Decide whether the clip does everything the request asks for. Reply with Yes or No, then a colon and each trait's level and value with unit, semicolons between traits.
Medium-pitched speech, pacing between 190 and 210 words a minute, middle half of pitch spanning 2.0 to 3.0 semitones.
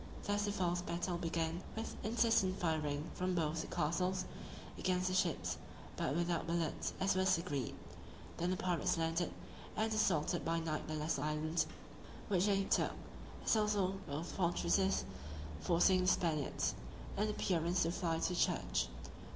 No: medium, 175 Hz; average, 150 wpm; narrow, 2.5 semitones